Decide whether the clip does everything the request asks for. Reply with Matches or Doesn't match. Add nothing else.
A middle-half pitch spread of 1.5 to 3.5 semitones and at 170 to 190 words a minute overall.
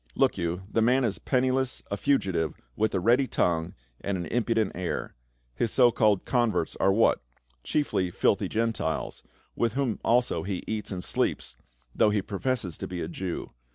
Doesn't match